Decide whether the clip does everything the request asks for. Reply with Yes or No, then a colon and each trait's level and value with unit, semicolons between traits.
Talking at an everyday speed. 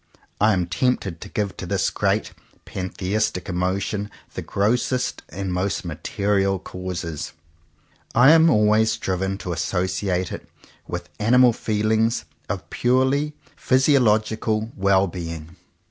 No: slow, 115 wpm